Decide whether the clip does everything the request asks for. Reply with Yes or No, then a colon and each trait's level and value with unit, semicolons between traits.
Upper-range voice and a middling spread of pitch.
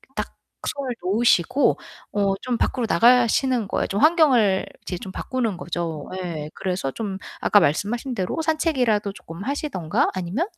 No: high, 210 Hz; wide, 5.7 semitones